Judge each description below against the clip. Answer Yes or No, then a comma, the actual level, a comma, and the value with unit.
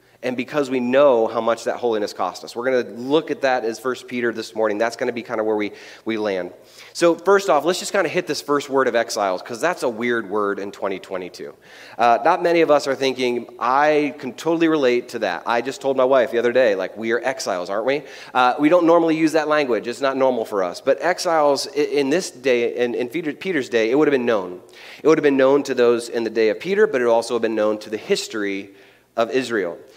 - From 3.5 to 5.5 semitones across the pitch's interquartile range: Yes, average, 4.9 semitones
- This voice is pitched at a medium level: No, low, 130 Hz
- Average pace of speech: No, fast, 250 wpm